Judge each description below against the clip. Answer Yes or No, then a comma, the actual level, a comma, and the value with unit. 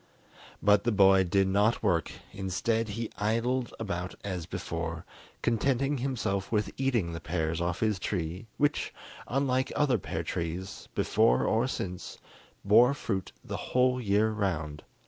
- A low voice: Yes, low, 105 Hz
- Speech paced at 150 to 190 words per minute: No, average, 140 wpm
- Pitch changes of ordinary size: Yes, average, 4.7 semitones